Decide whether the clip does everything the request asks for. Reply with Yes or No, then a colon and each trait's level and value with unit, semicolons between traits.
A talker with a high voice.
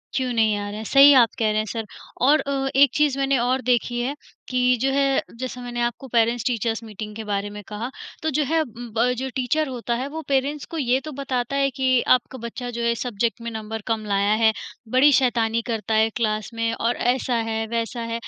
Yes: high, 240 Hz